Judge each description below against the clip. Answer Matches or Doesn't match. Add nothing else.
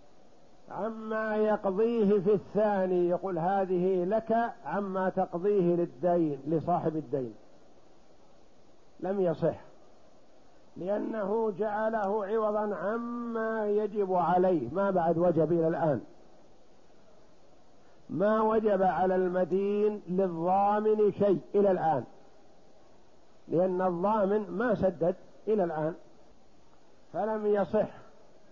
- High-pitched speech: Matches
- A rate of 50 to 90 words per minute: Matches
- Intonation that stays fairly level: Doesn't match